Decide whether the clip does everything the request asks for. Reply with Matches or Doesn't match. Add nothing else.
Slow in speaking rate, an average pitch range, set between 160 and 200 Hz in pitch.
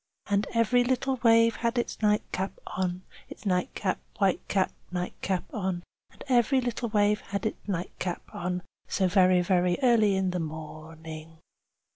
Doesn't match